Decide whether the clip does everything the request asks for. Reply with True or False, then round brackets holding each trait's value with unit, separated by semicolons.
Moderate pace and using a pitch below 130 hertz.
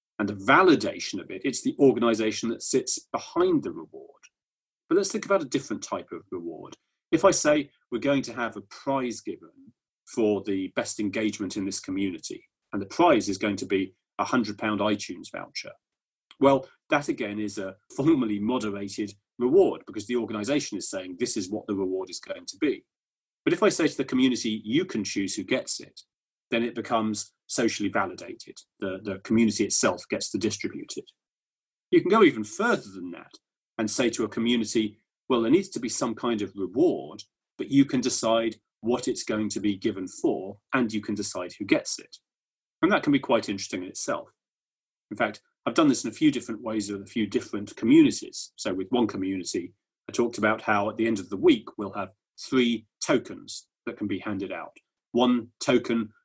True (195 wpm; 120 Hz)